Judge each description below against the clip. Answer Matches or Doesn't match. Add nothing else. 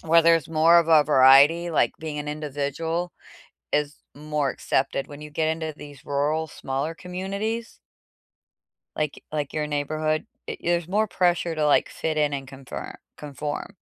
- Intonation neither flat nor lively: Doesn't match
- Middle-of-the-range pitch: Matches